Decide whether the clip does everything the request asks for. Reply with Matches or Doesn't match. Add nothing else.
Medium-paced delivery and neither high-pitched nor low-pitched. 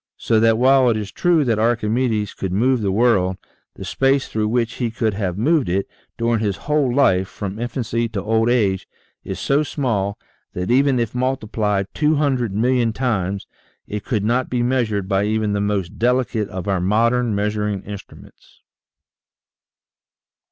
Doesn't match